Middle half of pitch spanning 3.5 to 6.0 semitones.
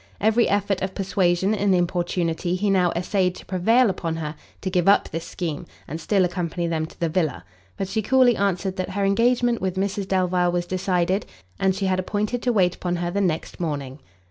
No: narrow, 2.4 semitones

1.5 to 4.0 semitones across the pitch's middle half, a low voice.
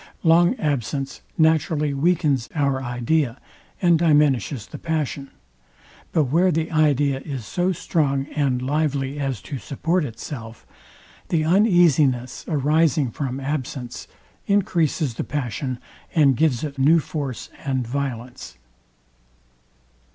No: average, 3.3 semitones; medium, 145 Hz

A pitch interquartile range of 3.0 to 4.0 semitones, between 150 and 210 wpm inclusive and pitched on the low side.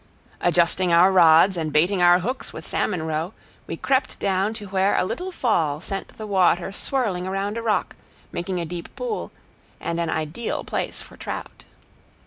No: average, 3.4 semitones; average, 170 wpm; medium, 185 Hz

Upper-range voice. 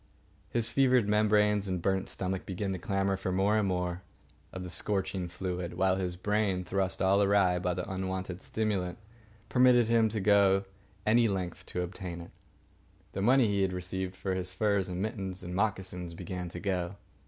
No: very low, 95 Hz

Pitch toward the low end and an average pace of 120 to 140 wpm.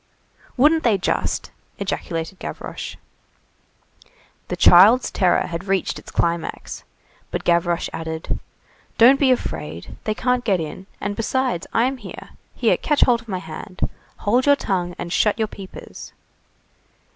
No: high, 200 Hz; slow, 135 wpm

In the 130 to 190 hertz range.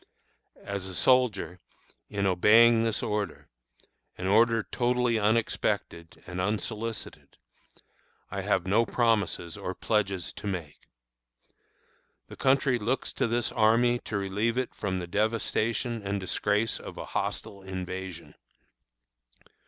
No: low, 105 Hz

